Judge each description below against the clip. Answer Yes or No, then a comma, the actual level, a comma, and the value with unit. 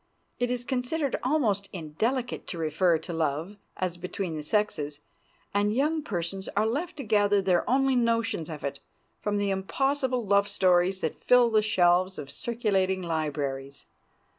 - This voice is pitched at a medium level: No, high, 200 Hz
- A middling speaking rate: Yes, average, 155 wpm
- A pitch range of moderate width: No, wide, 6.0 semitones